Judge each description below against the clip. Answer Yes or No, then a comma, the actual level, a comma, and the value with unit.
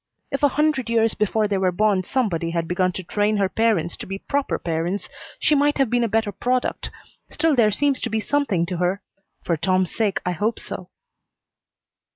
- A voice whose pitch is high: Yes, high, 210 Hz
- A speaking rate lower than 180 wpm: No, average, 195 wpm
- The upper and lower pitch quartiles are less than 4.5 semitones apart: No, average, 4.9 semitones